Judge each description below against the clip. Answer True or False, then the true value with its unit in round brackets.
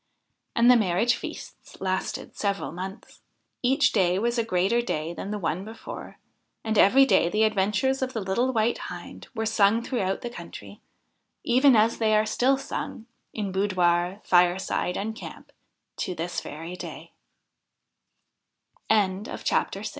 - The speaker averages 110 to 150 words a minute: True (140 wpm)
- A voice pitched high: True (210 Hz)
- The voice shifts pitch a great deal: False (4.0 semitones)